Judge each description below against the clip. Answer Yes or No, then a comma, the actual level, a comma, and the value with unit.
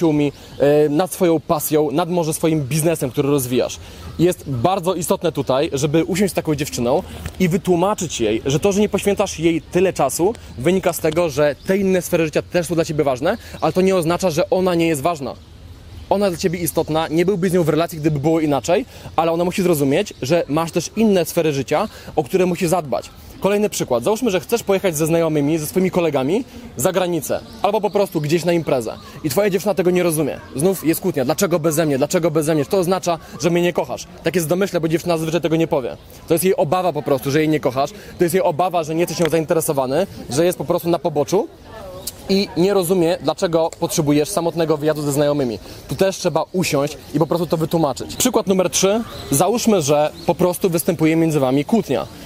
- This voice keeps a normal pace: No, fast, 210 wpm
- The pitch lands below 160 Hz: No, medium, 170 Hz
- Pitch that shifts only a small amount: No, average, 3.3 semitones